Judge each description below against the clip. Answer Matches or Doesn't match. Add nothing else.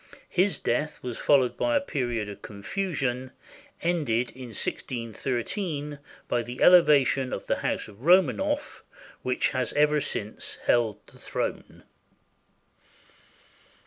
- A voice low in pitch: Matches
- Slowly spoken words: Matches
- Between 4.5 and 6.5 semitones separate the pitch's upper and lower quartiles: Matches